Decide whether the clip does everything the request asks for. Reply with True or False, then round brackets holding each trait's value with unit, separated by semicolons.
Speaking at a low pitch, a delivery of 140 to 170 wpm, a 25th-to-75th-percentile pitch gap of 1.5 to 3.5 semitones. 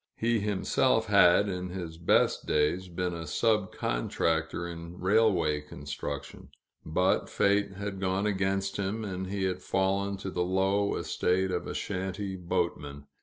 True (95 Hz; 145 wpm; 2.4 semitones)